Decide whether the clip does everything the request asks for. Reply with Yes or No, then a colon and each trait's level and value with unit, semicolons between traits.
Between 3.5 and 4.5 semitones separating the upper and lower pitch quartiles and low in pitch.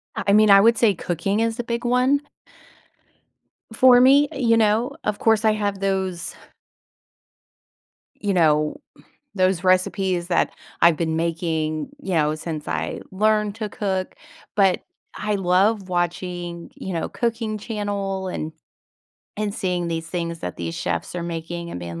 No: average, 4.0 semitones; high, 190 Hz